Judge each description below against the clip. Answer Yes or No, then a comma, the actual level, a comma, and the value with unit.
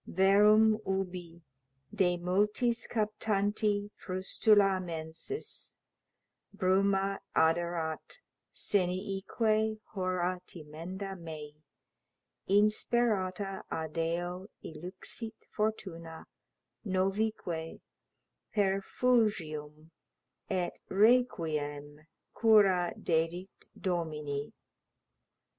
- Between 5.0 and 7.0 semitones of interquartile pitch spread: No, average, 4.0 semitones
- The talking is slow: Yes, slow, 55 wpm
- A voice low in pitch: No, medium, 185 Hz